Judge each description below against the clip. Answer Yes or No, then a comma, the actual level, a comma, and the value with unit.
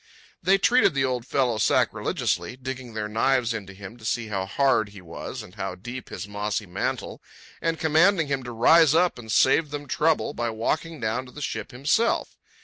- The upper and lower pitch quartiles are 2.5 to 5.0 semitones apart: No, wide, 5.4 semitones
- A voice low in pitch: Yes, low, 125 Hz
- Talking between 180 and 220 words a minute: Yes, average, 190 wpm